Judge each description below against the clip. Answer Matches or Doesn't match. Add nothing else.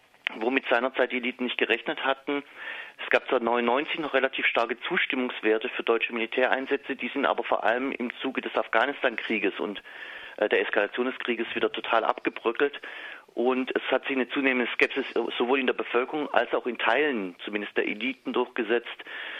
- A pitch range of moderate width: Doesn't match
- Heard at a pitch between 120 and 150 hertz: Matches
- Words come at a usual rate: Matches